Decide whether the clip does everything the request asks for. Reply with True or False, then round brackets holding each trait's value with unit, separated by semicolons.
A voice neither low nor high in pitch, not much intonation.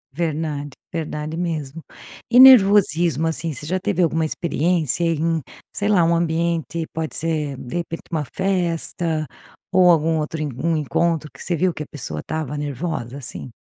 True (165 Hz; 2.2 semitones)